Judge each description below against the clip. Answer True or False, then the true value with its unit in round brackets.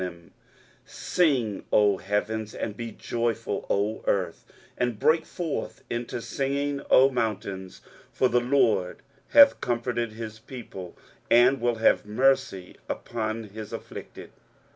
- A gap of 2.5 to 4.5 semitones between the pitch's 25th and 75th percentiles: True (3.6 semitones)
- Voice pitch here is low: True (115 Hz)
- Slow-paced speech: True (120 wpm)